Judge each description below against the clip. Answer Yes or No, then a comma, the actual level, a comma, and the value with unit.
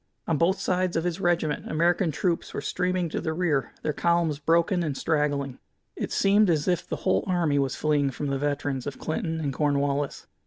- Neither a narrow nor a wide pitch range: Yes, average, 3.4 semitones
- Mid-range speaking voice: Yes, medium, 160 Hz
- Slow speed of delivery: No, average, 195 wpm